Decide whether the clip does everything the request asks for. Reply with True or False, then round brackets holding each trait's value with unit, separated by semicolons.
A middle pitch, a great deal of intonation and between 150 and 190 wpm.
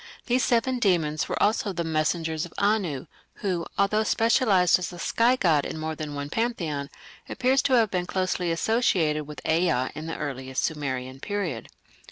True (175 Hz; 5.8 semitones; 170 wpm)